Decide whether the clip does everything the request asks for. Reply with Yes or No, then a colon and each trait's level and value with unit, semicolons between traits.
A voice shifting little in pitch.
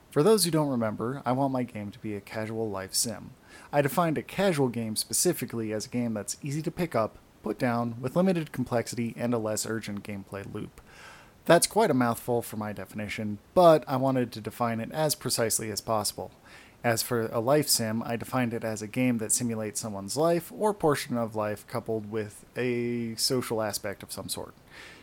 No: average, 3.2 semitones